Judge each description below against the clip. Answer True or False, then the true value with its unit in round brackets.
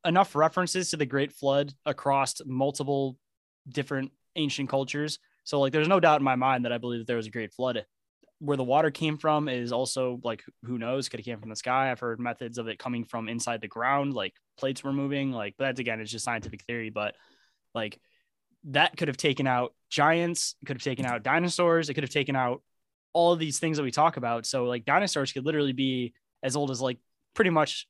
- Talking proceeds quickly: True (220 wpm)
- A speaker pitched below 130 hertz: False (135 Hz)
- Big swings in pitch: False (3.4 semitones)